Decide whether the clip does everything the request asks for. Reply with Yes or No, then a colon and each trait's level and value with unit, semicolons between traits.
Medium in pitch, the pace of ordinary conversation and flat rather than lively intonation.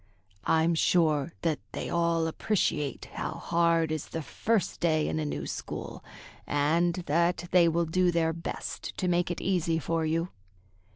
Yes: medium, 165 Hz; average, 160 wpm; narrow, 1.4 semitones